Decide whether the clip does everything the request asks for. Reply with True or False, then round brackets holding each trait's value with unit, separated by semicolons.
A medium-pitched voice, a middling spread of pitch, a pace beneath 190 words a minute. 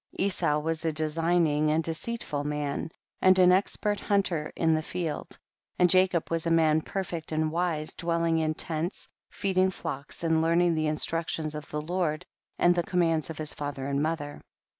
False (165 Hz; 2.3 semitones; 175 wpm)